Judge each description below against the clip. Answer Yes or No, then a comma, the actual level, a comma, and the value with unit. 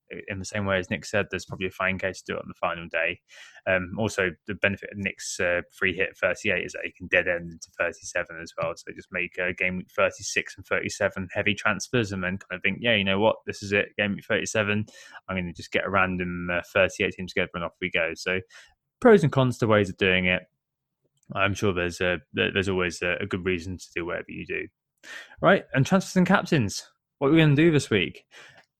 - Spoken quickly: Yes, fast, 245 wpm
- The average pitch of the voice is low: Yes, very low, 95 Hz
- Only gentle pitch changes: No, average, 3.0 semitones